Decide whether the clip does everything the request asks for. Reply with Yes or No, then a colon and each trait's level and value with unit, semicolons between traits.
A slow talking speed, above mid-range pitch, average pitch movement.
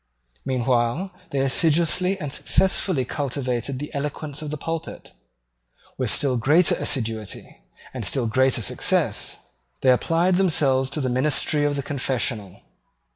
No: slow, 130 wpm; medium, 140 Hz; average, 3.5 semitones